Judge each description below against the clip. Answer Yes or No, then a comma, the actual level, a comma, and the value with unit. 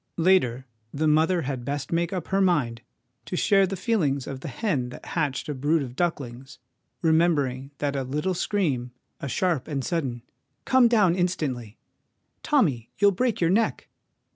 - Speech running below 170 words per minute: No, average, 175 wpm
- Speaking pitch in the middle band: Yes, medium, 155 Hz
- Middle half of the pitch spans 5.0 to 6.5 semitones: Yes, wide, 5.6 semitones